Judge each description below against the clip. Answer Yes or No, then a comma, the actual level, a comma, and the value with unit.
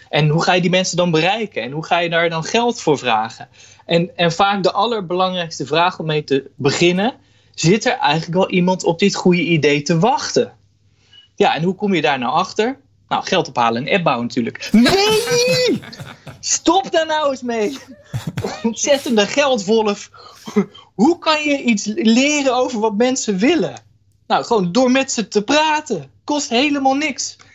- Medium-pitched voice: No, high, 200 Hz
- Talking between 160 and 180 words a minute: Yes, average, 175 wpm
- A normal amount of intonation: No, wide, 7.9 semitones